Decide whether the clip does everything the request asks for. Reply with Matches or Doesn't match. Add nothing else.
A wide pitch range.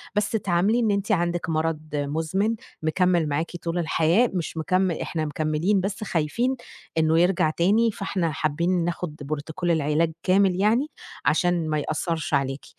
Doesn't match